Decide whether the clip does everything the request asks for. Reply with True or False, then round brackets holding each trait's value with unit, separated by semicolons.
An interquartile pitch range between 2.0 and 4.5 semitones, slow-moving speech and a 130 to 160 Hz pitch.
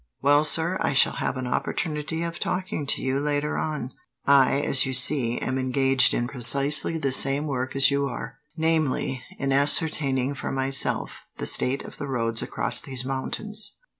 False (2.4 semitones; 170 wpm; 140 Hz)